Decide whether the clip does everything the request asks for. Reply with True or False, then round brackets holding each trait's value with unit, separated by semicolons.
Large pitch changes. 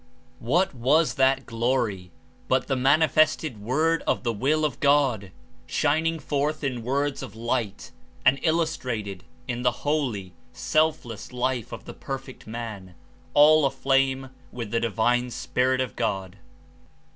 False (3.9 semitones)